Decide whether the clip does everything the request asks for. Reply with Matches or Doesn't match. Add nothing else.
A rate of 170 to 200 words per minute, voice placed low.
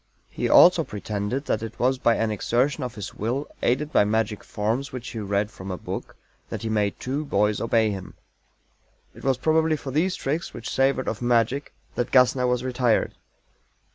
Matches